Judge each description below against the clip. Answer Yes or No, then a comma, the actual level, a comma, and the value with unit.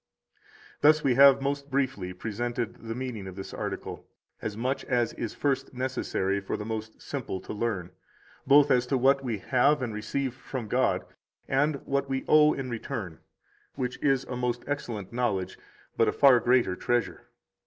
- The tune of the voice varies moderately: Yes, average, 3.6 semitones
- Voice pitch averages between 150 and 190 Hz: No, low, 125 Hz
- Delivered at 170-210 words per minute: Yes, average, 175 wpm